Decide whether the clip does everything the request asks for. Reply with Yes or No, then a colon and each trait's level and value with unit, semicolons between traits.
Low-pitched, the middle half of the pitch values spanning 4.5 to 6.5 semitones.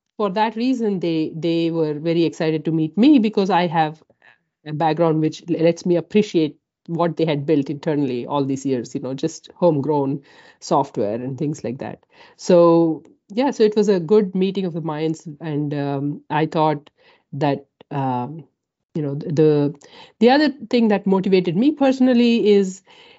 No: medium, 165 Hz; average, 5.2 semitones